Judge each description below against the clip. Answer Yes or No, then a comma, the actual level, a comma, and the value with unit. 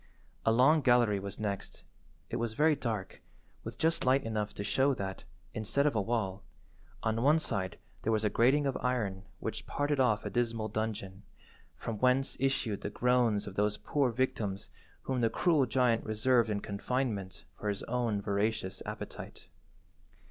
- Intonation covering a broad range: No, average, 3.8 semitones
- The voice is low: Yes, low, 115 Hz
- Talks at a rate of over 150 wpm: Yes, average, 165 wpm